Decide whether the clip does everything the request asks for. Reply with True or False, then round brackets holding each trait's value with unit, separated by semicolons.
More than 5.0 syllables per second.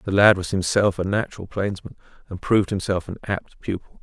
True (5.8 syllables/s)